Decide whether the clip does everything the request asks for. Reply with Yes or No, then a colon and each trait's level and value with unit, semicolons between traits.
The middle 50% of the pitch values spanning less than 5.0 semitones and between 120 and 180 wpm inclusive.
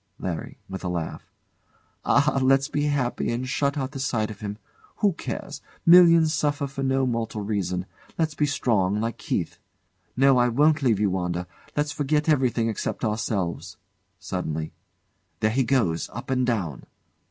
No: wide, 5.6 semitones; average, 160 wpm